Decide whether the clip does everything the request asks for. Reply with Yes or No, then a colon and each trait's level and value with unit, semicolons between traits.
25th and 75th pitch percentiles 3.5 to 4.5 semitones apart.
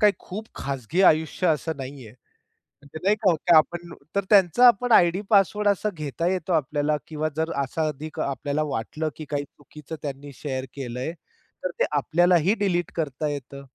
Yes: average, 4.1 semitones